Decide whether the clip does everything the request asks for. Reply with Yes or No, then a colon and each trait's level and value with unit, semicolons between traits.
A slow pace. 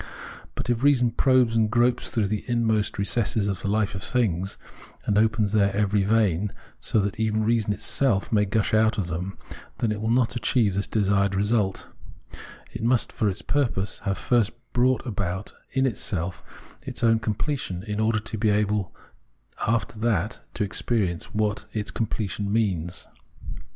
No: average, 165 wpm